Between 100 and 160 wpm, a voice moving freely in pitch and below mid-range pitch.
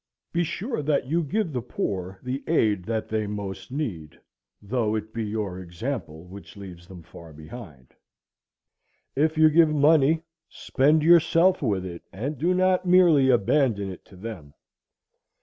Yes: average, 150 wpm; wide, 8.4 semitones; low, 115 Hz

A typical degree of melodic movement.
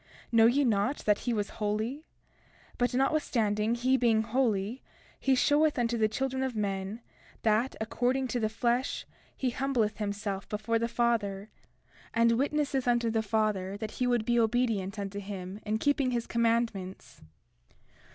Yes: average, 3.0 semitones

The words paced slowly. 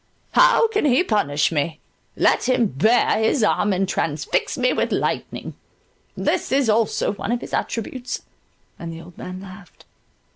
No: average, 145 wpm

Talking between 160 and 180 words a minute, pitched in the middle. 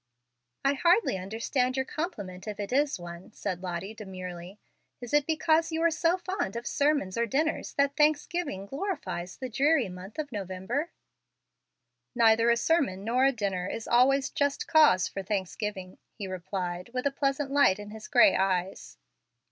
No: average, 165 wpm; high, 235 Hz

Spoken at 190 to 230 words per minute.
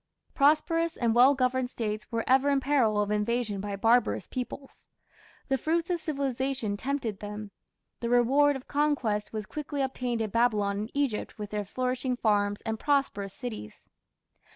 No: average, 155 wpm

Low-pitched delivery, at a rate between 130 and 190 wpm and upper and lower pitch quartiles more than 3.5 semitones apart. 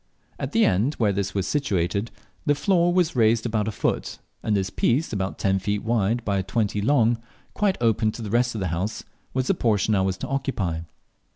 No: low, 110 Hz; fast, 205 wpm; average, 4.1 semitones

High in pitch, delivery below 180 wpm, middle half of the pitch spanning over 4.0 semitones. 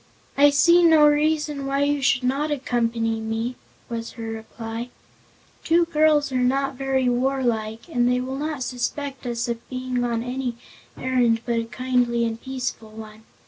No: very high, 255 Hz; average, 160 wpm; average, 3.1 semitones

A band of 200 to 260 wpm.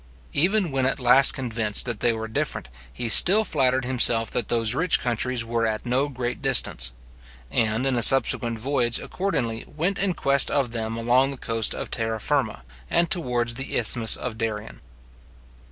No: average, 170 wpm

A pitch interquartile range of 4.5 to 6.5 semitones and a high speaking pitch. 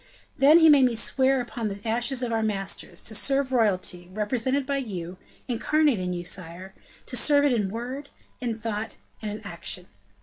Yes: average, 5.0 semitones; high, 230 Hz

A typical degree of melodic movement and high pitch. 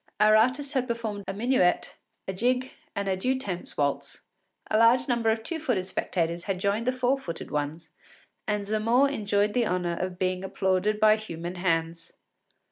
Yes: average, 4.7 semitones; high, 205 Hz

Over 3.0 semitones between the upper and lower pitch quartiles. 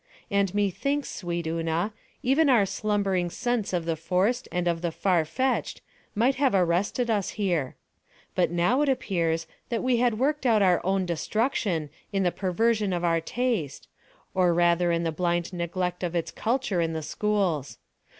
Yes: average, 4.6 semitones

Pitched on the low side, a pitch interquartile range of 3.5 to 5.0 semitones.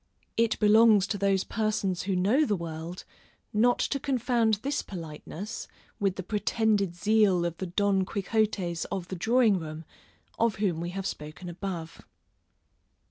No: high, 195 Hz; average, 3.8 semitones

